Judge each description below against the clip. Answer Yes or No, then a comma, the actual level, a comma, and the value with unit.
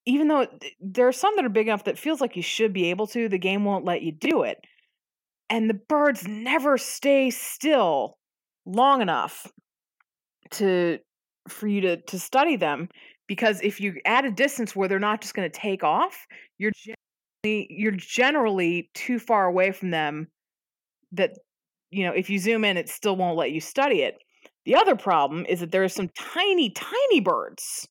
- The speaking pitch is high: Yes, high, 215 Hz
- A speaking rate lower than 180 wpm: No, average, 185 wpm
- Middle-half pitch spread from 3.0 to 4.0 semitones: No, wide, 5.6 semitones